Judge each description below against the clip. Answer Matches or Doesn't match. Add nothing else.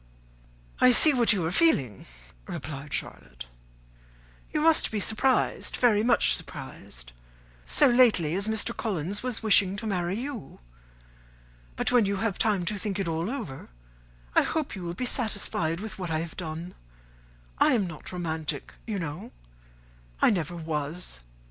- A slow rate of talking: Doesn't match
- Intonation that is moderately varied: Doesn't match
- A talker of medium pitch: Doesn't match